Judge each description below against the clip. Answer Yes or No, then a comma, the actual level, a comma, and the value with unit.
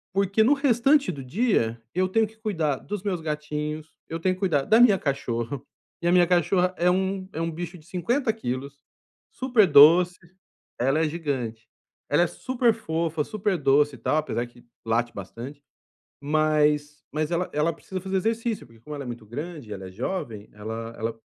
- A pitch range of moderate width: No, wide, 5.7 semitones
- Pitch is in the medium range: Yes, medium, 160 Hz